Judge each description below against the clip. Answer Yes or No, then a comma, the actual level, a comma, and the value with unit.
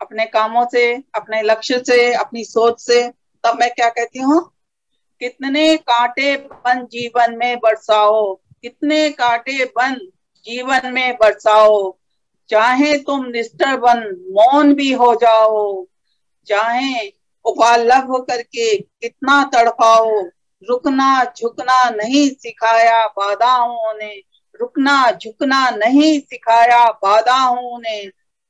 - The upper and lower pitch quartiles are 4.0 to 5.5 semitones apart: No, average, 3.1 semitones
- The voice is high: Yes, high, 240 Hz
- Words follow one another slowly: Yes, slow, 105 wpm